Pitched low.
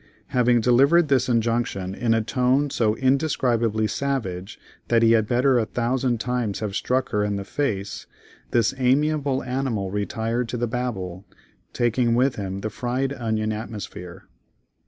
Yes: low, 120 Hz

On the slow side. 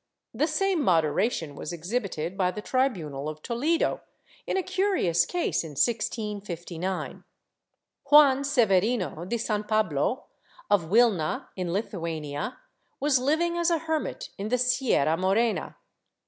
Yes: slow, 130 wpm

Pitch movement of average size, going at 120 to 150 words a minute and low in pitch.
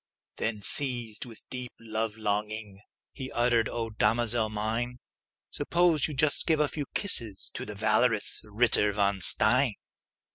Yes: average, 3.0 semitones; average, 145 wpm; low, 115 Hz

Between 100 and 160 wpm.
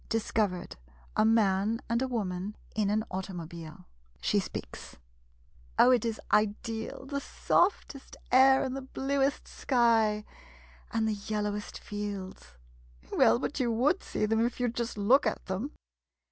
Yes: average, 155 wpm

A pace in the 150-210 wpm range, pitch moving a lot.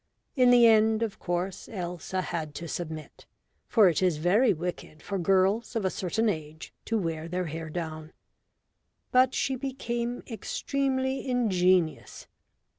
No: average, 140 wpm; wide, 5.8 semitones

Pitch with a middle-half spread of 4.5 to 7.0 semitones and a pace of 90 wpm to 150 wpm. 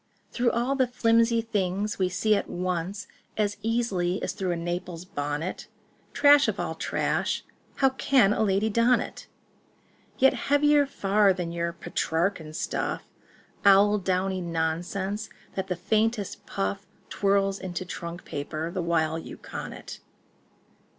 No: average, 4.1 semitones; slow, 135 wpm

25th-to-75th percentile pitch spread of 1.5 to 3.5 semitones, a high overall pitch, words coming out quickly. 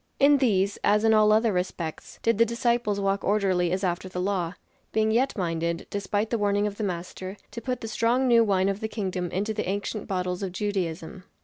Yes: average, 2.9 semitones; high, 200 Hz; fast, 210 wpm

